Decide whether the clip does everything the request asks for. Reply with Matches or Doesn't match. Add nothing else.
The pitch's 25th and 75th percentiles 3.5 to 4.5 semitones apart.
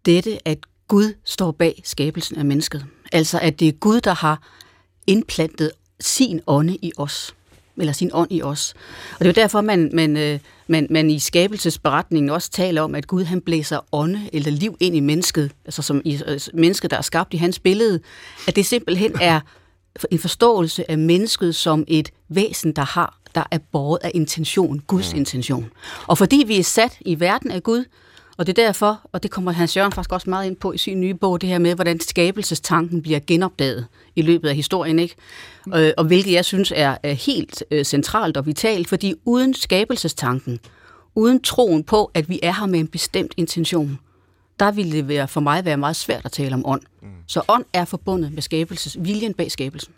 Matches